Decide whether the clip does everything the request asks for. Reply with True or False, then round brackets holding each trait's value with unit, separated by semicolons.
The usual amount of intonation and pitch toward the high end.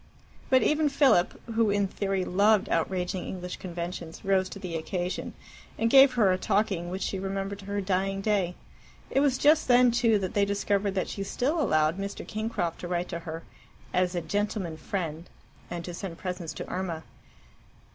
True (3.0 semitones; 195 Hz)